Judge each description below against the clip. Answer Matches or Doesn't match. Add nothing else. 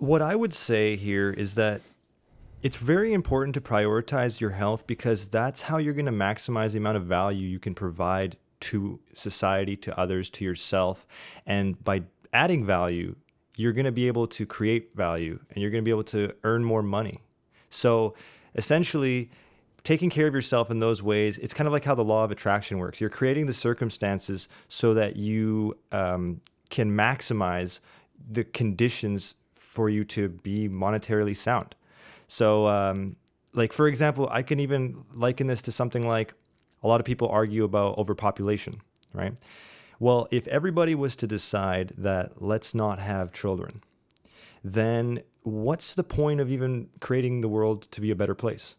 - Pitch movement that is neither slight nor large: Matches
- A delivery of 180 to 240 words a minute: Doesn't match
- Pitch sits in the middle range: Doesn't match